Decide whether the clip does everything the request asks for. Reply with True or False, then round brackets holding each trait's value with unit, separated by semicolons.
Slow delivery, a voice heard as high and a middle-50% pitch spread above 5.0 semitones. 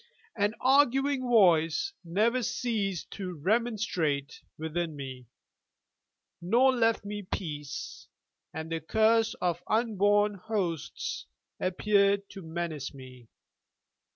True (100 wpm; 195 Hz; 5.6 semitones)